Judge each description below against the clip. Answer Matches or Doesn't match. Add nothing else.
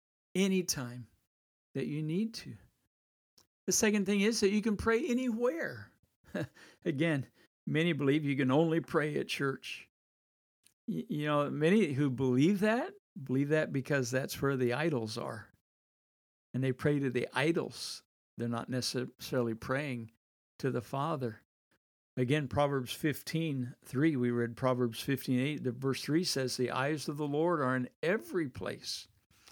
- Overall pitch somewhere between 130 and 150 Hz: Matches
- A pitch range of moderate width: Matches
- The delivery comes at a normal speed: Matches